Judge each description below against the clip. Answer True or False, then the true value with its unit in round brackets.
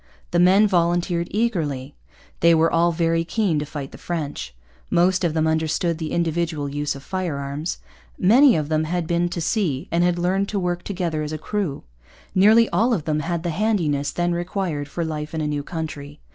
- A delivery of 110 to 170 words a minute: False (195 wpm)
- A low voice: False (170 Hz)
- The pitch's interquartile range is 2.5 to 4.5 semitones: True (2.8 semitones)